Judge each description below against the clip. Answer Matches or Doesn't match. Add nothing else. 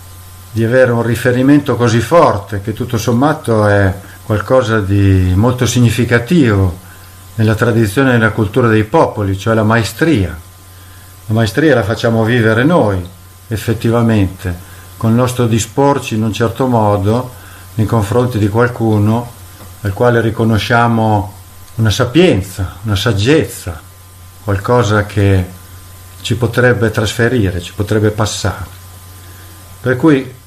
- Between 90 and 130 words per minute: Matches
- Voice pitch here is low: Matches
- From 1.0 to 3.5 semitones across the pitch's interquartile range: Doesn't match